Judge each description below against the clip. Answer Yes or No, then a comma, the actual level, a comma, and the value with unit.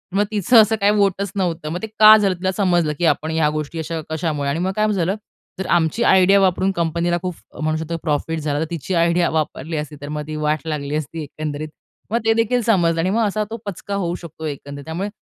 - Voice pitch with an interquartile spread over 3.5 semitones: Yes, average, 4.1 semitones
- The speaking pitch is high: No, medium, 170 Hz